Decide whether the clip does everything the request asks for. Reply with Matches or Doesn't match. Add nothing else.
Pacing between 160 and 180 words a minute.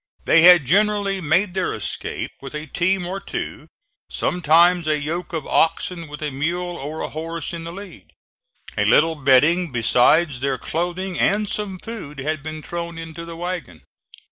Matches